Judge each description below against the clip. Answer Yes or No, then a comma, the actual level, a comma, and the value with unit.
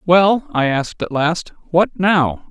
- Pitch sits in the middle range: Yes, medium, 170 Hz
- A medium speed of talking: Yes, average, 170 wpm